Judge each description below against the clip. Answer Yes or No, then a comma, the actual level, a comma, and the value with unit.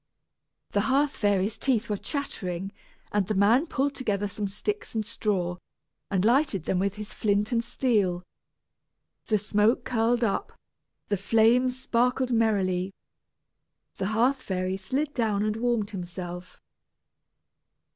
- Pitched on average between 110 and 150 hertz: No, high, 215 Hz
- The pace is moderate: No, slow, 130 wpm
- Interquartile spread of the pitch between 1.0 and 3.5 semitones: No, average, 3.9 semitones